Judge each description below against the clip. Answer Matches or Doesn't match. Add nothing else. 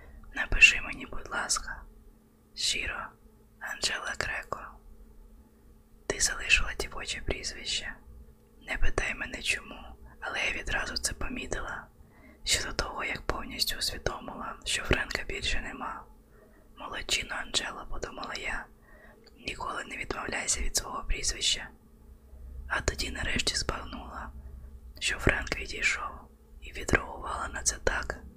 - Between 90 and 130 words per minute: Matches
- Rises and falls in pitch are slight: Matches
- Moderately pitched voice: Doesn't match